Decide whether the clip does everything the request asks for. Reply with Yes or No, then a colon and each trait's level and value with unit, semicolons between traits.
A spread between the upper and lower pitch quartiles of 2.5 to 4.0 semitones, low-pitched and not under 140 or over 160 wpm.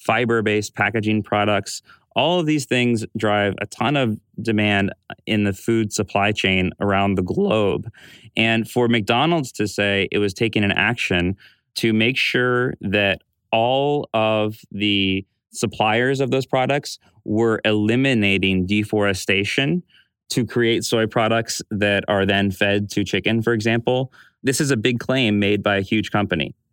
Yes: average, 2.8 semitones; low, 110 Hz; average, 150 wpm